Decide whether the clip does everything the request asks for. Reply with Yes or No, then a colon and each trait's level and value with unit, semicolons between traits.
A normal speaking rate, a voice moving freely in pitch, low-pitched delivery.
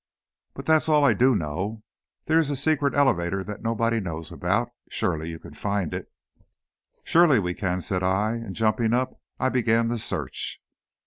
Yes: average, 175 wpm; wide, 5.9 semitones; low, 110 Hz